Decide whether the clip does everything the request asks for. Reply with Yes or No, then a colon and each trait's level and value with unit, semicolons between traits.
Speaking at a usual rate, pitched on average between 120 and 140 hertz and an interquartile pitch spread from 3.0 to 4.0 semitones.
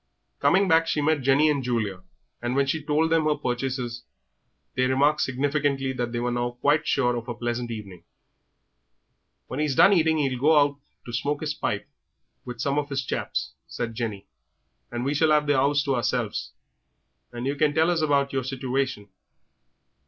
Yes: average, 185 wpm; low, 135 Hz; average, 3.4 semitones